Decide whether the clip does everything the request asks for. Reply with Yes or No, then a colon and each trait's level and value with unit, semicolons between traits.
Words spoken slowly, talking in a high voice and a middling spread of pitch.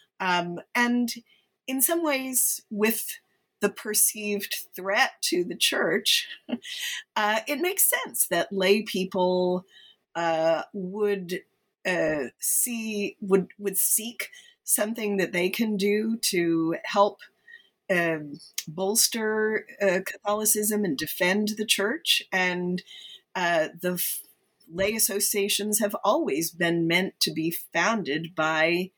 Yes: slow, 115 wpm; high, 205 Hz; average, 4.1 semitones